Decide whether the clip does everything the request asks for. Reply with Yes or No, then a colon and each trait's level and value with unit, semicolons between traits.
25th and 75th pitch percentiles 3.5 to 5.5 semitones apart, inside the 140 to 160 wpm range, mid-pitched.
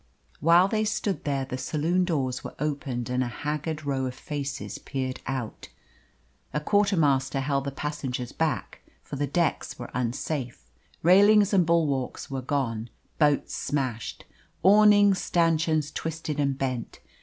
Yes: average, 4.1 semitones; average, 145 wpm; medium, 145 Hz